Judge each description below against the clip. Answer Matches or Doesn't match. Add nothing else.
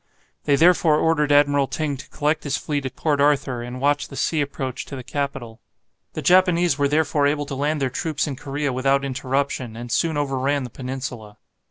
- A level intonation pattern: Matches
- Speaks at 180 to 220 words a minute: Matches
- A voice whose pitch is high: Doesn't match